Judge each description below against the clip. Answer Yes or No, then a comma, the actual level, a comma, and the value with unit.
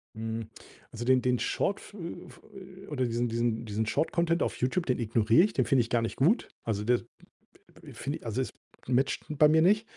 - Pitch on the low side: Yes, low, 125 Hz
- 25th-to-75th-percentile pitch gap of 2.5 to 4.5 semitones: No, wide, 5.4 semitones